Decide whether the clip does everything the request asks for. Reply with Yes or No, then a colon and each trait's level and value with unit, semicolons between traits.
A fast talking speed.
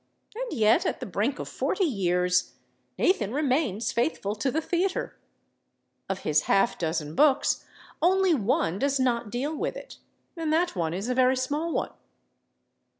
No: average, 155 wpm